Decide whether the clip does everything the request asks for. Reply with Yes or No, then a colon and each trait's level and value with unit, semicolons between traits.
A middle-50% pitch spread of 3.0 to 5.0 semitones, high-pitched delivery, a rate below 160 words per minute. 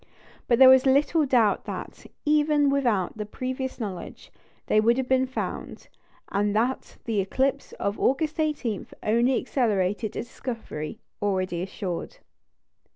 Yes: average, 4.4 semitones; high, 240 Hz; slow, 135 wpm